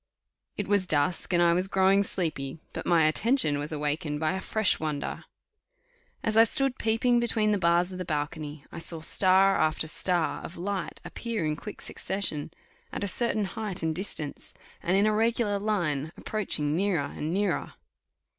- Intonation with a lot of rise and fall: No, average, 4.8 semitones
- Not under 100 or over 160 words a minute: No, average, 175 wpm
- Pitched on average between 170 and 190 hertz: Yes, medium, 185 Hz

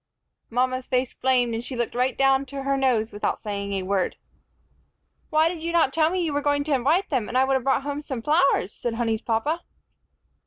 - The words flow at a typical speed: No, fast, 220 wpm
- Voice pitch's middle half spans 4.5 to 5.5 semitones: No, average, 3.5 semitones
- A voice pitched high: Yes, very high, 265 Hz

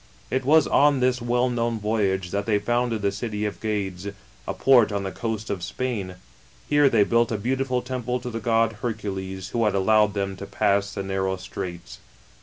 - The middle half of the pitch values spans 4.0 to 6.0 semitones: No, average, 3.6 semitones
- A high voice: No, low, 110 Hz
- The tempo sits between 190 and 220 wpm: Yes, average, 195 wpm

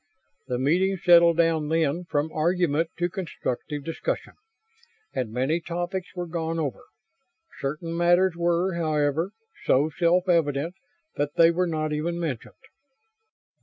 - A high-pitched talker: No, medium, 165 Hz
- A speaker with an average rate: No, slow, 130 wpm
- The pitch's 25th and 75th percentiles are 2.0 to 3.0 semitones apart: Yes, narrow, 2.5 semitones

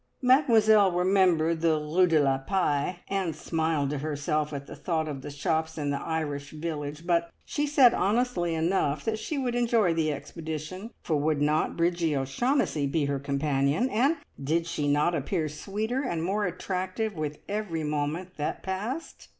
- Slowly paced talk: No, average, 165 wpm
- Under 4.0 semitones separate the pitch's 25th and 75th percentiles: No, average, 4.6 semitones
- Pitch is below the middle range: No, medium, 165 Hz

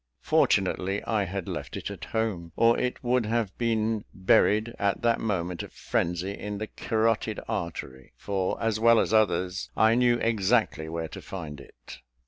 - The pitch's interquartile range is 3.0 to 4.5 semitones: Yes, average, 3.8 semitones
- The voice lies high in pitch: No, low, 105 Hz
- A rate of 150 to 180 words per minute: Yes, average, 165 wpm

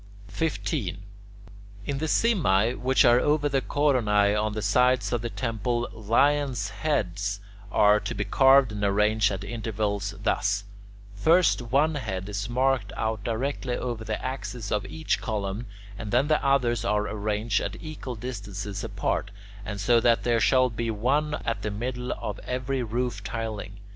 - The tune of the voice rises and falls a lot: No, average, 3.8 semitones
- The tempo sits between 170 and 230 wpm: No, average, 160 wpm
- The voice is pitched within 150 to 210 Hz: No, low, 115 Hz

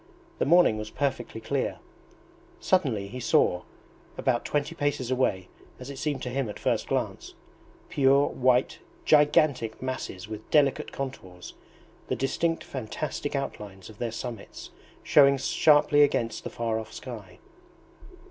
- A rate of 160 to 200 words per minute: No, slow, 135 wpm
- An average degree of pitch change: Yes, average, 4.3 semitones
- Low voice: Yes, low, 130 Hz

